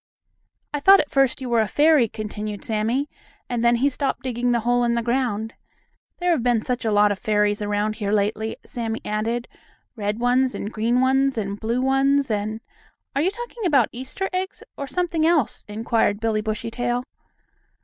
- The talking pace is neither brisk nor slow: Yes, average, 185 wpm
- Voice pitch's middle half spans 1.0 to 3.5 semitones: No, average, 3.9 semitones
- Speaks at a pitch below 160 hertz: No, high, 235 Hz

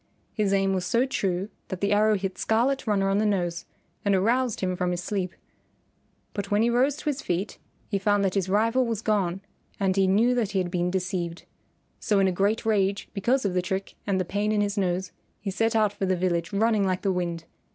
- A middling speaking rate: No, fast, 225 wpm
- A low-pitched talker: No, high, 195 Hz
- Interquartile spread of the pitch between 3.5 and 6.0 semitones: No, narrow, 2.6 semitones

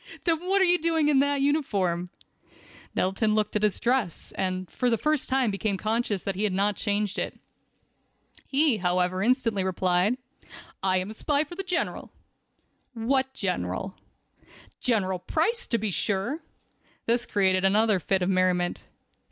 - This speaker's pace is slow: No, average, 155 wpm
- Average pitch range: No, wide, 6.1 semitones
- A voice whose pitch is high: Yes, high, 210 Hz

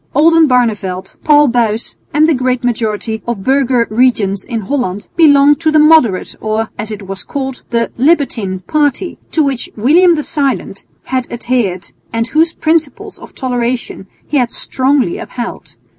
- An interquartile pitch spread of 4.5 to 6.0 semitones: Yes, average, 4.9 semitones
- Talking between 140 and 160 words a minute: Yes, average, 150 wpm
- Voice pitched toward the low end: No, very high, 250 Hz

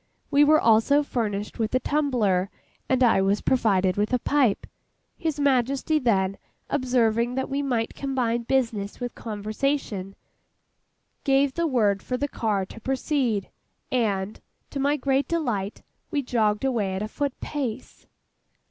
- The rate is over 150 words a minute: No, average, 145 wpm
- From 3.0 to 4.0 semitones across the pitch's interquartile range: No, average, 4.7 semitones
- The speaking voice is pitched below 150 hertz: No, high, 245 Hz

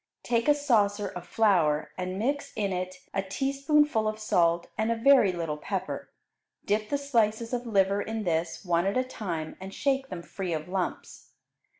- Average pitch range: Yes, average, 4.6 semitones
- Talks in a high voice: Yes, high, 205 Hz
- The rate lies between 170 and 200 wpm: Yes, average, 180 wpm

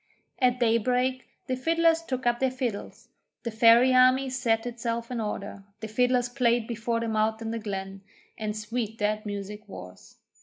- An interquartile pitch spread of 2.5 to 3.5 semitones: Yes, average, 2.8 semitones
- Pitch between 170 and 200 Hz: No, high, 230 Hz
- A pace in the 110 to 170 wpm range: Yes, average, 165 wpm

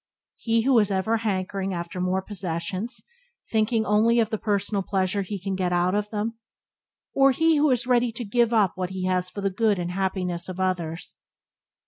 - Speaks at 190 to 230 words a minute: Yes, average, 195 wpm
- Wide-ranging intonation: No, average, 3.5 semitones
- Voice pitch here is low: No, high, 200 Hz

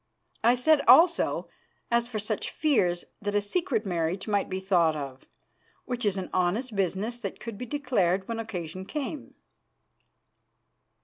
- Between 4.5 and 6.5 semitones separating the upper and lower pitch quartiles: Yes, average, 4.8 semitones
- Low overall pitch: No, high, 205 Hz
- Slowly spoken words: No, average, 145 wpm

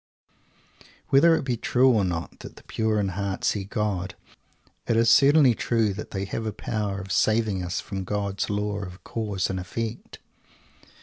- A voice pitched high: No, low, 105 Hz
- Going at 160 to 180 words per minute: Yes, average, 175 wpm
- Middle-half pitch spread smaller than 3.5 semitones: Yes, average, 2.9 semitones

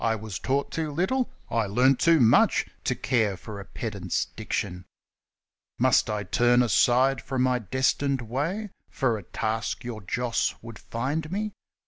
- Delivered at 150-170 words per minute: Yes, average, 165 wpm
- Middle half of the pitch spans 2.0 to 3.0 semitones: No, average, 4.0 semitones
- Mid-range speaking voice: No, low, 120 Hz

